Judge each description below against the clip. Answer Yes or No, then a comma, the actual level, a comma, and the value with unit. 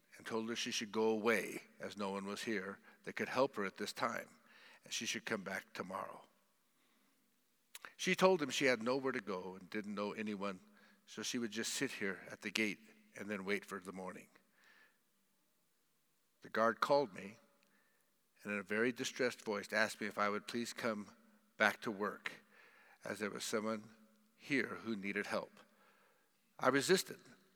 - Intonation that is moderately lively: No, narrow, 2.3 semitones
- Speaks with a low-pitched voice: Yes, low, 110 Hz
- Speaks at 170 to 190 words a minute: Yes, average, 180 wpm